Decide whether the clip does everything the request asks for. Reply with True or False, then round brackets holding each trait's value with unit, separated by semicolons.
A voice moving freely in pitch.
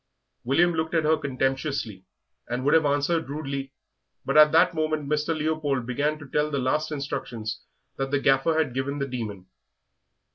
False (2.7 semitones)